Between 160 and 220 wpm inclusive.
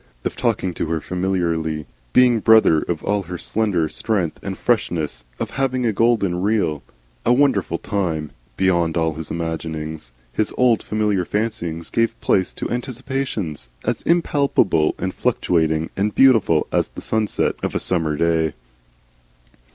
No: average, 145 wpm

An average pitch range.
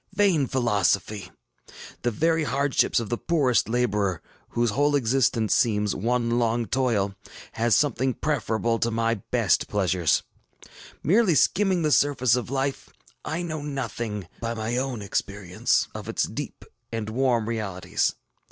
Yes: average, 4.3 semitones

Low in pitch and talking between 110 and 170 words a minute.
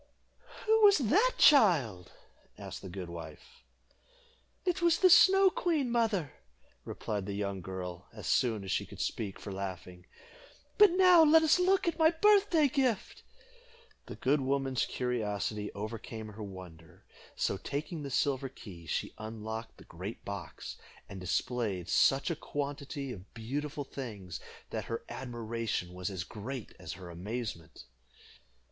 Yes: low, 120 Hz; average, 145 wpm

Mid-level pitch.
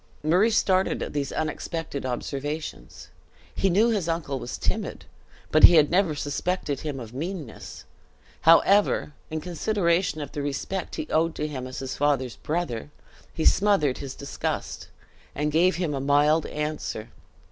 Yes: medium, 155 Hz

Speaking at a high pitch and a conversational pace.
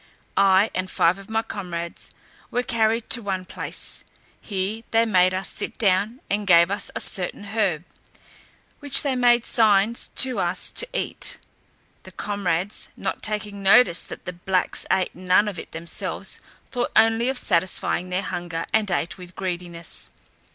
Yes: high, 195 Hz; average, 160 wpm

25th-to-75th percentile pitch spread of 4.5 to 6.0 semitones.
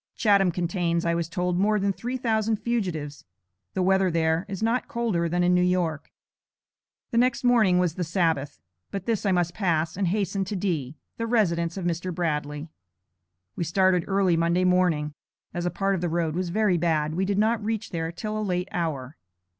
No: average, 3.1 semitones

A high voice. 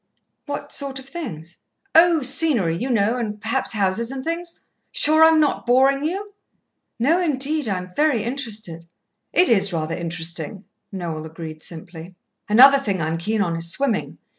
Yes: high, 230 Hz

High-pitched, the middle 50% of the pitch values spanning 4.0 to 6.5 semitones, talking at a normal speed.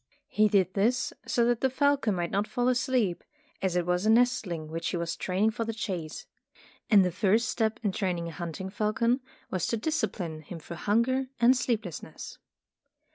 Yes: high, 210 Hz; average, 5.2 semitones; average, 185 wpm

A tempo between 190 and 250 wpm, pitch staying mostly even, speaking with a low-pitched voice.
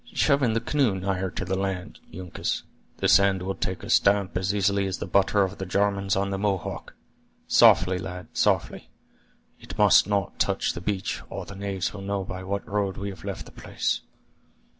Yes: average, 195 wpm; narrow, 1.2 semitones; very low, 95 Hz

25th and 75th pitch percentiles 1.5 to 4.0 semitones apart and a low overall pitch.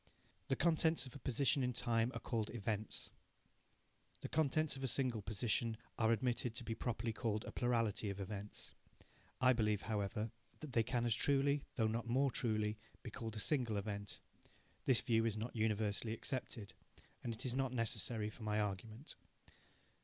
Yes: average, 2.9 semitones; low, 115 Hz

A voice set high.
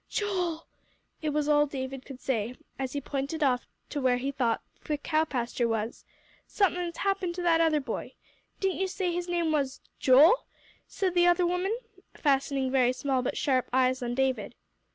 Yes: very high, 290 Hz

